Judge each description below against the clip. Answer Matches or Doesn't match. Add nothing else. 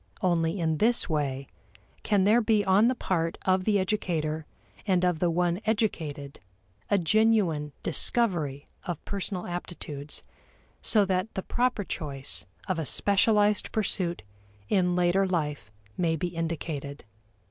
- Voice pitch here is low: Doesn't match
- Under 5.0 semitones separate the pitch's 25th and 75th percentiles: Matches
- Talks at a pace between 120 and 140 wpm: Matches